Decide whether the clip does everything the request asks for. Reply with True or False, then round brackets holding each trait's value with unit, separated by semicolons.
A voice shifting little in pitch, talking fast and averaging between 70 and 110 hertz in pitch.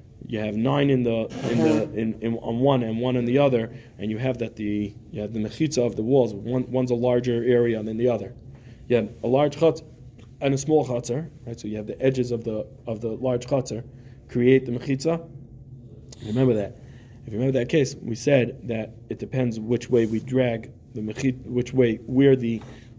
False (2.3 semitones; 215 wpm; 120 Hz)